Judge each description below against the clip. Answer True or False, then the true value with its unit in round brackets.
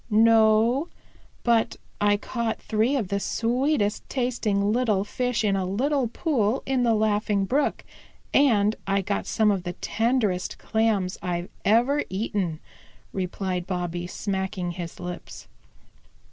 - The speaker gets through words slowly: True (130 wpm)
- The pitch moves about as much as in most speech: True (3.7 semitones)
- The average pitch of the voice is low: False (215 Hz)